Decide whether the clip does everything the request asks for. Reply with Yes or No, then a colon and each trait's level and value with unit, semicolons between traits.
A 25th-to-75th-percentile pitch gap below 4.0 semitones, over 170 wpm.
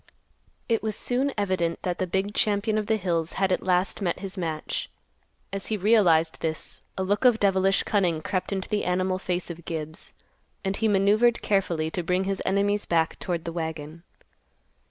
Yes: average, 3.2 semitones; average, 180 wpm